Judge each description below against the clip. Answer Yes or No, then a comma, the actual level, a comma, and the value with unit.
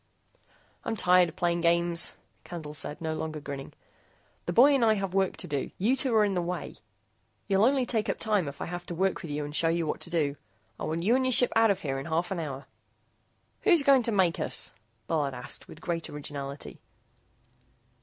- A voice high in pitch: No, medium, 175 Hz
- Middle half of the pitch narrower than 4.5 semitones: No, average, 5.3 semitones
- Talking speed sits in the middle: No, fast, 215 wpm